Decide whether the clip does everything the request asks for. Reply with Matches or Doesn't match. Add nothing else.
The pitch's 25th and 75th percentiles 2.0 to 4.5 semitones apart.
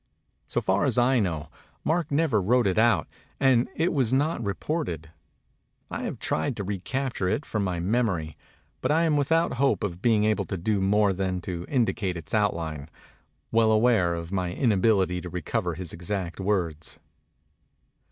Doesn't match